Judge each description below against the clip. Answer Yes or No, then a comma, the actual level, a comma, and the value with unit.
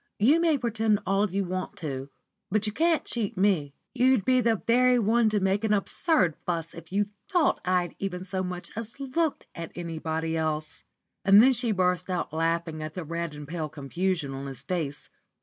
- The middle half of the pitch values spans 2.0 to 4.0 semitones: No, wide, 5.5 semitones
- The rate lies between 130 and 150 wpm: No, average, 195 wpm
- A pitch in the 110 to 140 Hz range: No, medium, 185 Hz